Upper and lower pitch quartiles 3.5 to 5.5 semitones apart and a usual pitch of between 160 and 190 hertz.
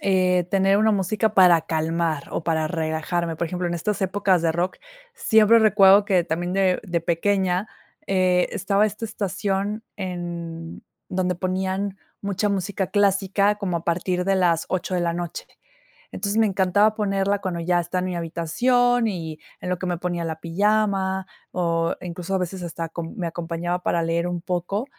No: narrow, 2.6 semitones; medium, 185 Hz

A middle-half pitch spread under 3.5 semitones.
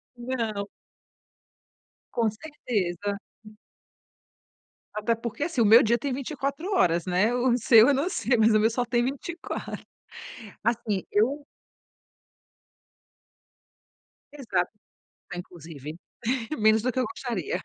No: average, 3.9 semitones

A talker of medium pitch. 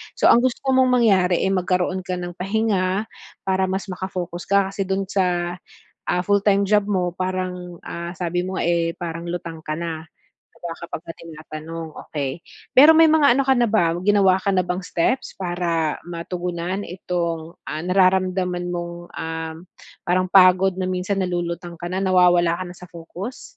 Yes: medium, 180 Hz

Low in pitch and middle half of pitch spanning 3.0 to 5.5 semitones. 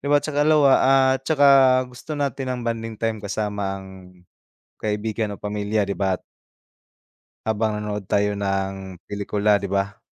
No: low, 105 Hz; narrow, 2.6 semitones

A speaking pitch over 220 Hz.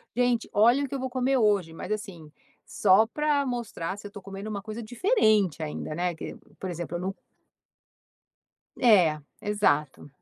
No: high, 205 Hz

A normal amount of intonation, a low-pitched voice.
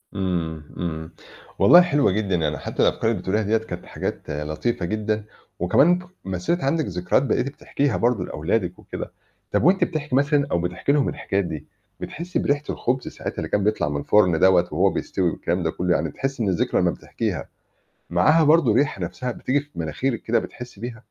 No: wide, 7.7 semitones; low, 105 Hz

